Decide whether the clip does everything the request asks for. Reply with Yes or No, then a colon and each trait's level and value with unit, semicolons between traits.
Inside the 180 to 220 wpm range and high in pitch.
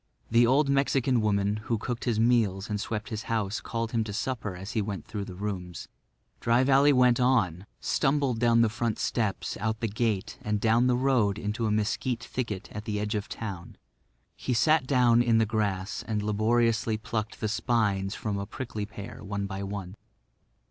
No: average, 190 wpm; low, 110 Hz